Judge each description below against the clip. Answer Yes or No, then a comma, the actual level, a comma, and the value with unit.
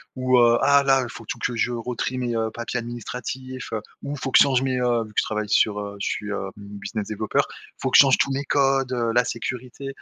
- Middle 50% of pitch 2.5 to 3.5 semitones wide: Yes, average, 2.8 semitones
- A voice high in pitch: No, low, 120 Hz